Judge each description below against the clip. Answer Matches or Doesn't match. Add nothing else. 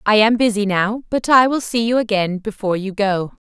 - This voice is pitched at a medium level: Doesn't match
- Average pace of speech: Doesn't match